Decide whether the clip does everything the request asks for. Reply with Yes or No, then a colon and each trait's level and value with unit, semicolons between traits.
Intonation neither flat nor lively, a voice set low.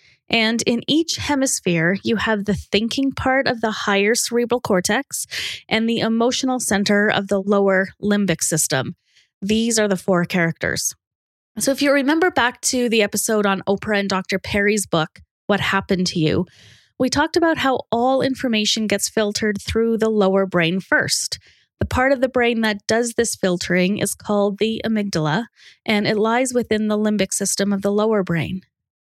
No: average, 3.3 semitones; high, 210 Hz